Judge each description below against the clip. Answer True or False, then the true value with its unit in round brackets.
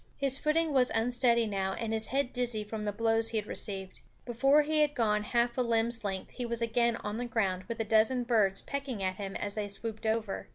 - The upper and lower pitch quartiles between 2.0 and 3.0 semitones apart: True (2.7 semitones)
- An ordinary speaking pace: False (230 wpm)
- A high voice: True (225 Hz)